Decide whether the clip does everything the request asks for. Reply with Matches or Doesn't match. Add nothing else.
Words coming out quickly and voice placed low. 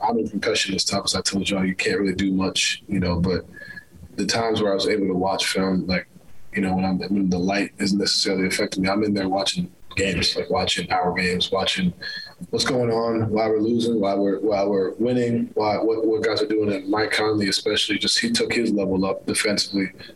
Matches